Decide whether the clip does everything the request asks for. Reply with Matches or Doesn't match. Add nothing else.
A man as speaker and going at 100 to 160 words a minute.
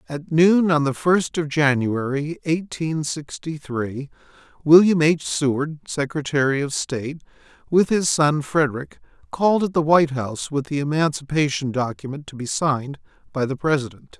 Matches